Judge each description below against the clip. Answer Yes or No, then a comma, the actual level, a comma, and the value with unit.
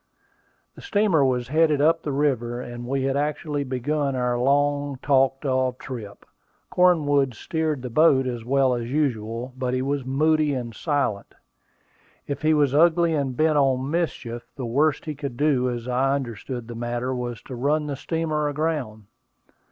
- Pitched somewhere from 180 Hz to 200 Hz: No, low, 135 Hz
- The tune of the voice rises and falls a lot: No, average, 3.3 semitones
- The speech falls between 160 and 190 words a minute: Yes, average, 165 wpm